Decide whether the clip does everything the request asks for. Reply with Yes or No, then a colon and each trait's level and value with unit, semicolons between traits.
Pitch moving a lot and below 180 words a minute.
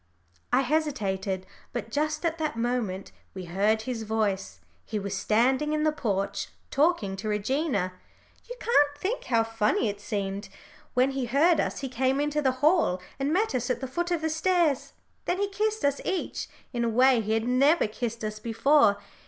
No: wide, 6.2 semitones; average, 185 wpm